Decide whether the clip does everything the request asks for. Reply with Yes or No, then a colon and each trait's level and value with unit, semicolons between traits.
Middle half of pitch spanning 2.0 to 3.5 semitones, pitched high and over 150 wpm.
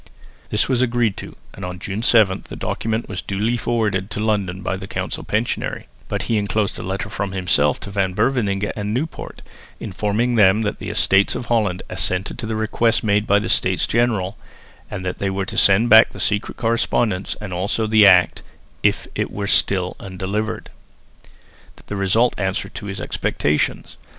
No: average, 2.7 semitones; low, 105 Hz; average, 180 wpm